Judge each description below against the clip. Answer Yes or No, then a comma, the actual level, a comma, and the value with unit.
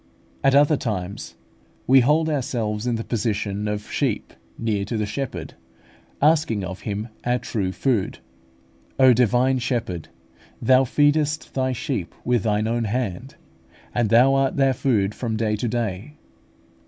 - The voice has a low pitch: Yes, low, 120 Hz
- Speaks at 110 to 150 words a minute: Yes, average, 145 wpm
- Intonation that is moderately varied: Yes, average, 4.0 semitones